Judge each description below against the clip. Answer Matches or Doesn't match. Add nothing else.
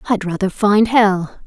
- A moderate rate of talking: Matches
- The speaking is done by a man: Doesn't match